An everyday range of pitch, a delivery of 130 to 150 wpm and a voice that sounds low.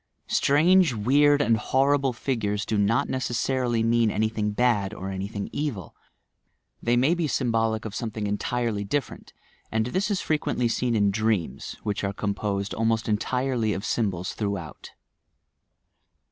Yes: average, 3.8 semitones; average, 145 wpm; low, 115 Hz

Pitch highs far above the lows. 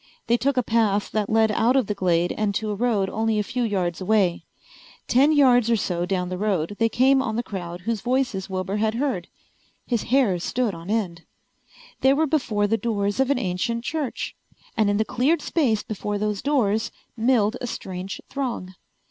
No: average, 4.1 semitones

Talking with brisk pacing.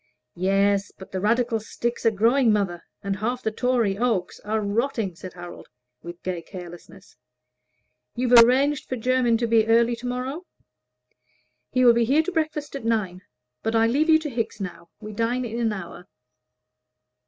No: average, 170 wpm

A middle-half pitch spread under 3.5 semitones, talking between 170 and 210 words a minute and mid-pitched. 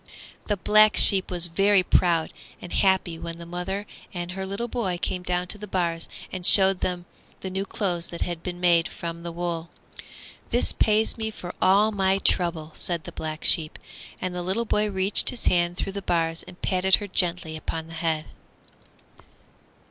Yes: narrow, 2.4 semitones; average, 180 wpm; medium, 180 Hz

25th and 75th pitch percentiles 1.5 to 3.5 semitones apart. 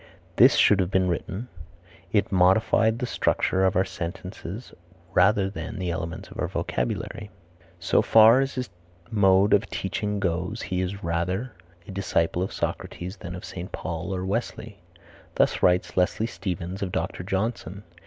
Yes: narrow, 2.6 semitones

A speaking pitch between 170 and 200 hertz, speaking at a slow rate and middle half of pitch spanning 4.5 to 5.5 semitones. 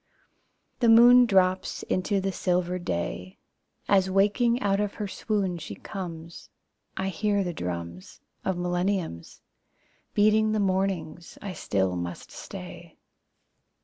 No: high, 190 Hz; slow, 120 wpm; average, 3.3 semitones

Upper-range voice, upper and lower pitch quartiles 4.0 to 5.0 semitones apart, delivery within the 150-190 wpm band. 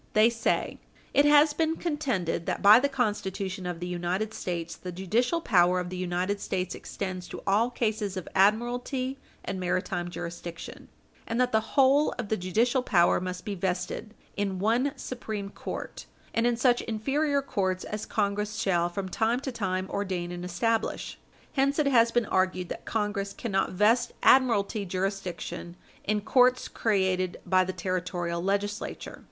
Yes: high, 205 Hz; average, 4.4 semitones; average, 160 wpm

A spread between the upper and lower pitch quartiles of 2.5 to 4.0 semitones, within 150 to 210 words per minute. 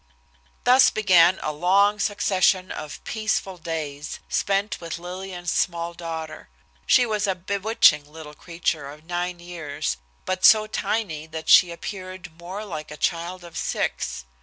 No: average, 3.2 semitones; average, 140 wpm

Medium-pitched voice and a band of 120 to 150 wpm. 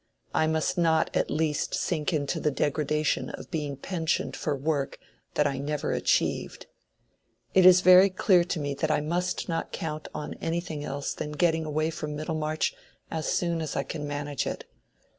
No: medium, 155 Hz; average, 175 wpm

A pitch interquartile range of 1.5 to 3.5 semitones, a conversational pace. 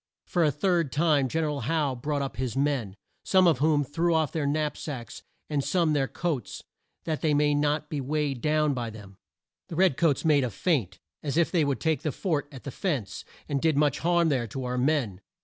No: average, 3.0 semitones; fast, 220 wpm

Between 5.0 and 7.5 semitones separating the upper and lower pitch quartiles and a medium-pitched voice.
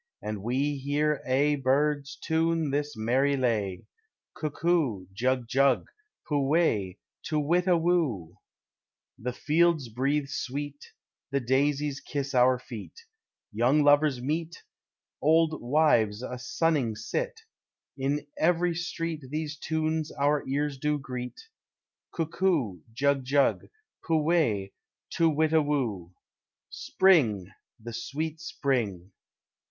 No: average, 4.0 semitones; medium, 145 Hz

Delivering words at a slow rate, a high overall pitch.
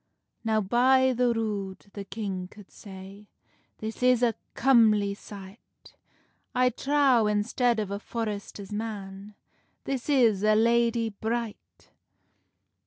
Yes: slow, 115 wpm; high, 220 Hz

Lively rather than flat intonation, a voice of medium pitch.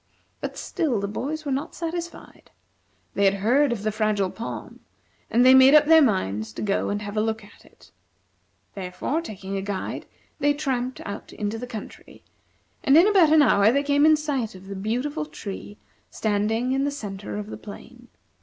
No: wide, 6.0 semitones; high, 230 Hz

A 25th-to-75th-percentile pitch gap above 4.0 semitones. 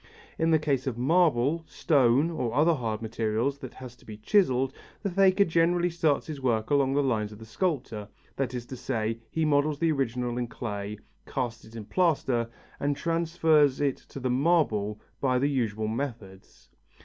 Yes: average, 5.3 semitones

